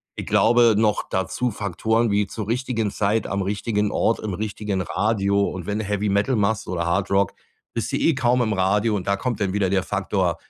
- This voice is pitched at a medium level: No, low, 105 Hz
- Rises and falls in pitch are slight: Yes, narrow, 2.2 semitones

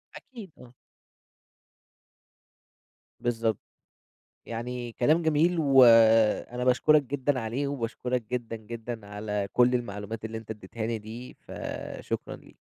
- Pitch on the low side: Yes, low, 120 Hz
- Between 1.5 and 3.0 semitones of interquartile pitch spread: Yes, narrow, 2.4 semitones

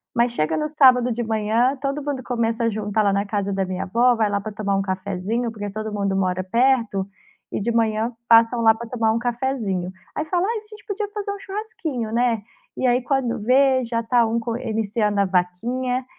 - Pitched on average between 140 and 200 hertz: No, high, 230 Hz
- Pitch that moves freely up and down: No, average, 3.7 semitones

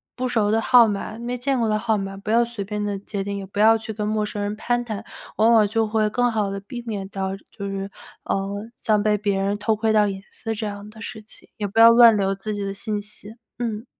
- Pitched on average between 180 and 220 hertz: Yes, high, 210 Hz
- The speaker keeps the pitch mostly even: Yes, narrow, 1.9 semitones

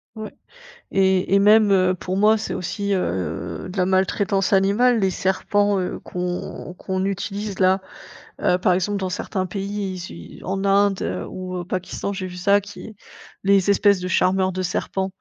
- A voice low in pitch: No, high, 190 Hz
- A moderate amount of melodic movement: No, narrow, 1.5 semitones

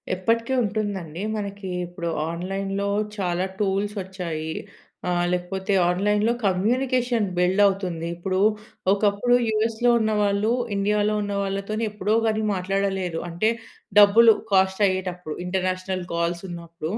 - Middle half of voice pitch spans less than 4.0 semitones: Yes, narrow, 2.6 semitones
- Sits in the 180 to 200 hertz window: Yes, high, 195 Hz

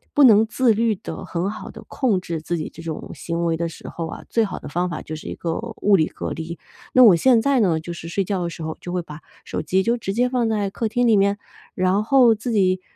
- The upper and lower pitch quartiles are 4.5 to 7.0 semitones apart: Yes, average, 4.9 semitones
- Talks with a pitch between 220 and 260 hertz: No, high, 195 Hz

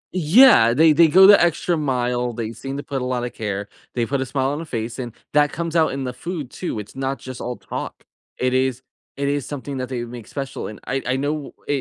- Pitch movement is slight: No, average, 3.3 semitones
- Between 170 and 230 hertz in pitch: No, low, 135 Hz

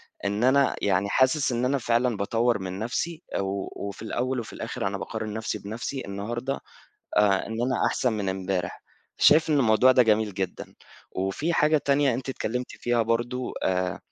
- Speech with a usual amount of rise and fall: Yes, average, 4.3 semitones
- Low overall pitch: Yes, low, 115 Hz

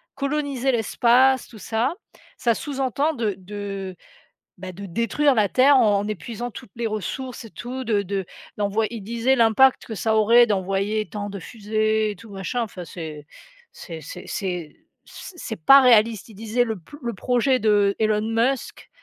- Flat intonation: No, average, 3.4 semitones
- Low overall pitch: No, high, 220 Hz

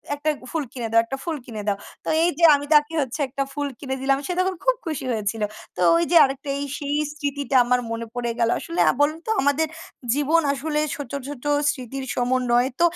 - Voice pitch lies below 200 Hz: No, very high, 280 Hz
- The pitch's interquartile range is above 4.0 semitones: No, average, 3.4 semitones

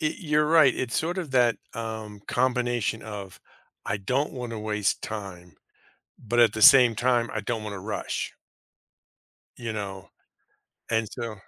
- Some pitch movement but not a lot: Yes, average, 3.2 semitones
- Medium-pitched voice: No, low, 115 Hz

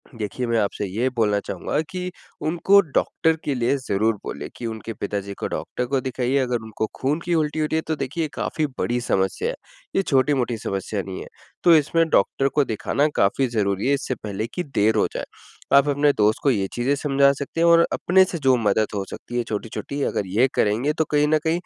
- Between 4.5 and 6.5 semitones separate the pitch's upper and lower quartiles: Yes, wide, 5.5 semitones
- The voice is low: Yes, low, 130 Hz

